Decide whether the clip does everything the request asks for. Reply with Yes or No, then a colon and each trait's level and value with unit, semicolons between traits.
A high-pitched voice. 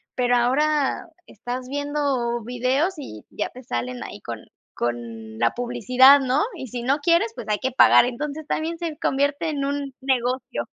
Yes: very high, 260 Hz